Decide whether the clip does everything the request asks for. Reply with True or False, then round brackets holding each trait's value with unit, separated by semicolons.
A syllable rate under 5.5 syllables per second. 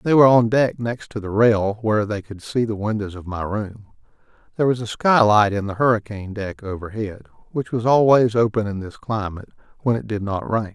False (5.7 syllables/s)